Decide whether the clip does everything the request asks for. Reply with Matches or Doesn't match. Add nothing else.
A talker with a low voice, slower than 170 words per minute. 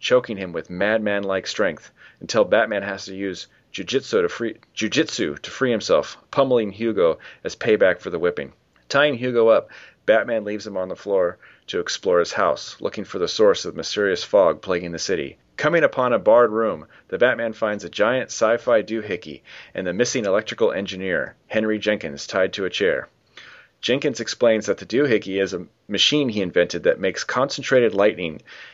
Doesn't match